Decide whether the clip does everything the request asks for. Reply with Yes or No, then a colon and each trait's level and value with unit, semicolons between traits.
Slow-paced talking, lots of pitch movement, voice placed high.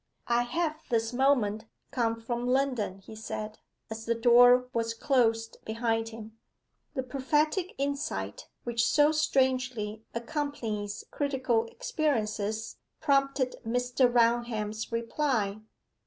No: slow, 110 wpm; average, 3.2 semitones; high, 240 Hz